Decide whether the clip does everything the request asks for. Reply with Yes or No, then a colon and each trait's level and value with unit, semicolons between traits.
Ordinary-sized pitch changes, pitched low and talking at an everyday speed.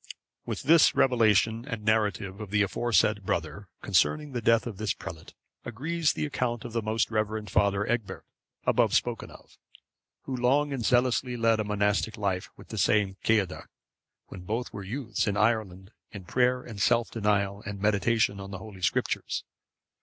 Yes: average, 3.0 semitones; low, 110 Hz; average, 170 wpm